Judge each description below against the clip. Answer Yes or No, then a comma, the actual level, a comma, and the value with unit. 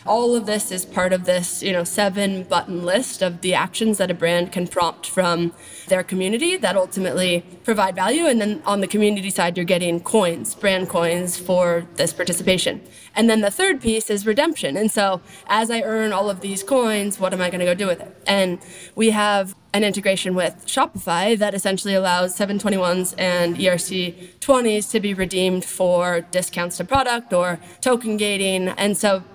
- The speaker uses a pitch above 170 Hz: Yes, high, 190 Hz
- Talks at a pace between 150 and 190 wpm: Yes, average, 185 wpm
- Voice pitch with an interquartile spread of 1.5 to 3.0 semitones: Yes, average, 2.7 semitones